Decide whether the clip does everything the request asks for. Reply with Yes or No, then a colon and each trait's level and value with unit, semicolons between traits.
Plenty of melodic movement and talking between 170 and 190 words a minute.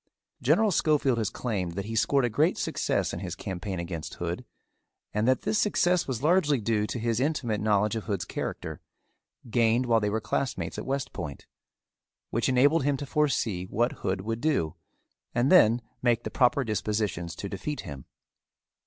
No: average, 4.8 semitones; average, 175 wpm